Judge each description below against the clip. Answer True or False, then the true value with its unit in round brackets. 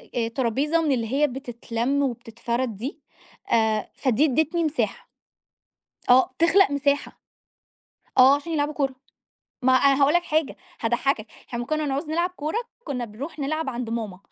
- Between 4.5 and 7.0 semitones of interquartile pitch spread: False (4.1 semitones)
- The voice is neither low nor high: False (275 Hz)